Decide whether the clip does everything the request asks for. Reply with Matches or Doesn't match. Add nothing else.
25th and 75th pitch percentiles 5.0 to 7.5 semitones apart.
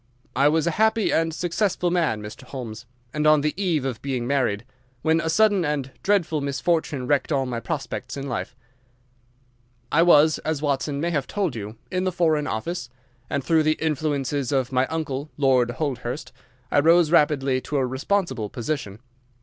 Doesn't match